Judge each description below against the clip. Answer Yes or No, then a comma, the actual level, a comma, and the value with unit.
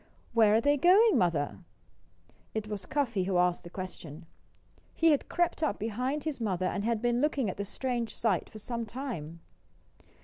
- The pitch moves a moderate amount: No, wide, 6.3 semitones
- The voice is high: Yes, high, 225 Hz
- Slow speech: No, average, 175 wpm